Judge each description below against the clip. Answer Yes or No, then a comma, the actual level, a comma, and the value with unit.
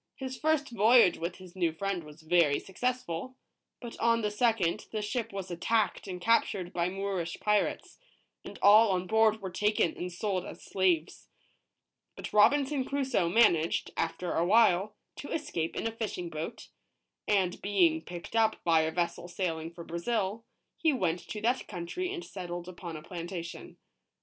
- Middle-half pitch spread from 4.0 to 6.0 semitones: Yes, average, 4.7 semitones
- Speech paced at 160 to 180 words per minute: Yes, average, 170 wpm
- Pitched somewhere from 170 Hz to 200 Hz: Yes, high, 190 Hz